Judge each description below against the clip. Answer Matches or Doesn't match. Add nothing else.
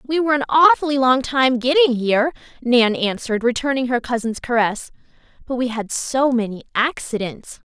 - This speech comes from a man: Doesn't match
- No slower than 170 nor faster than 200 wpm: Doesn't match